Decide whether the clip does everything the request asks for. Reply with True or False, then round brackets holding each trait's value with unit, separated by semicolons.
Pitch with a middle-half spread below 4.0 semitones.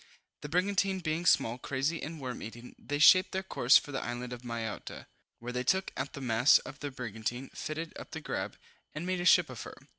False (5.4 semitones)